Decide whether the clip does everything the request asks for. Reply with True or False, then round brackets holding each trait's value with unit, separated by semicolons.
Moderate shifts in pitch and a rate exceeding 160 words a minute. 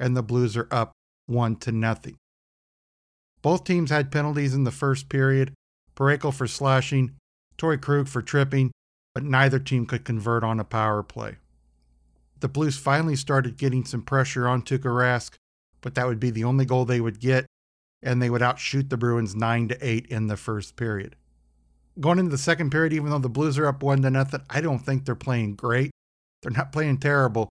True (3.2 semitones; 185 wpm)